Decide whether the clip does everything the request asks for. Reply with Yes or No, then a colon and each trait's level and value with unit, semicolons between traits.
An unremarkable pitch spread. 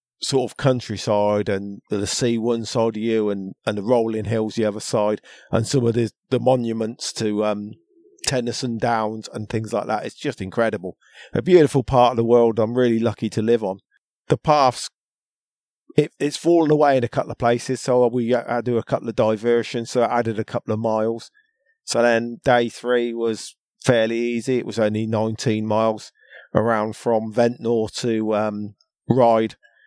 No: narrow, 2.1 semitones